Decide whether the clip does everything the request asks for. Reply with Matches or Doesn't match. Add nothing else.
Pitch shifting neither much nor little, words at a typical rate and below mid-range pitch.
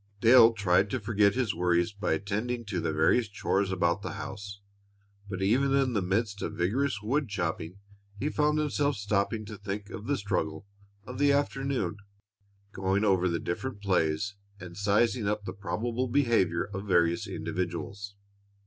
Matches